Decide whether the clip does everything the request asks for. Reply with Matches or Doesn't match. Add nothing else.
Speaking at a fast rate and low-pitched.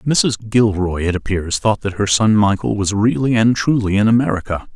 Doesn't match